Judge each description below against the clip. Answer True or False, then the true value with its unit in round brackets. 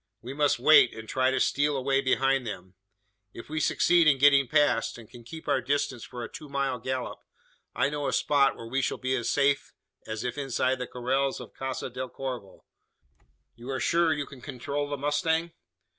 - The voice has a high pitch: False (135 Hz)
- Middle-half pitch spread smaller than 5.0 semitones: True (2.5 semitones)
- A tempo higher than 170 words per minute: True (200 wpm)